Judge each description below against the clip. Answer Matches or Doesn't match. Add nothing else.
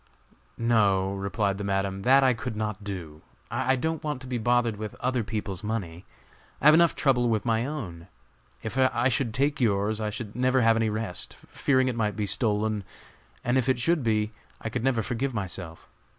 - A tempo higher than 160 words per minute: Matches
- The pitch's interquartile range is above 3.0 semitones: Matches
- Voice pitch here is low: Matches